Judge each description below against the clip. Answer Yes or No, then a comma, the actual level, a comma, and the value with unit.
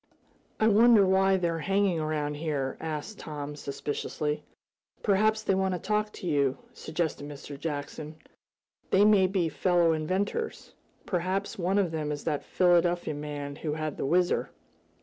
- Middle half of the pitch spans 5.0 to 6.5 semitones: No, average, 4.3 semitones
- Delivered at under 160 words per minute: Yes, average, 150 wpm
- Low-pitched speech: No, medium, 170 Hz